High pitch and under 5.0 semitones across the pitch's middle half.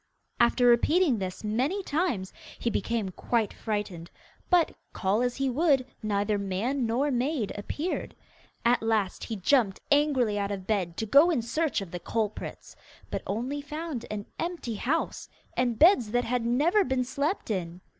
No: high, 240 Hz; wide, 5.6 semitones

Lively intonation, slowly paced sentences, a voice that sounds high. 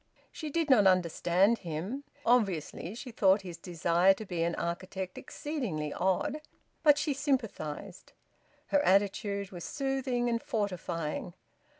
Yes: wide, 6.2 semitones; slow, 125 wpm; high, 195 Hz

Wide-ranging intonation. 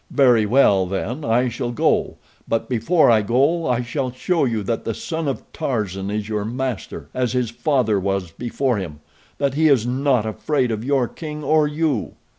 No: average, 4.5 semitones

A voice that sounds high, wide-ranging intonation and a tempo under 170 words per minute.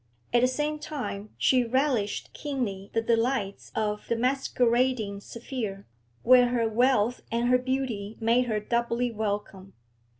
No: high, 235 Hz; average, 3.2 semitones; slow, 135 wpm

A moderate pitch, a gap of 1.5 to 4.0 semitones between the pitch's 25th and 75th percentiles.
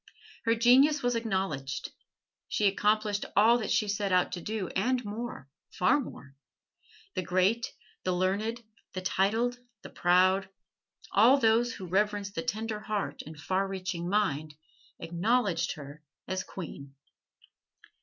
No: high, 200 Hz; average, 3.7 semitones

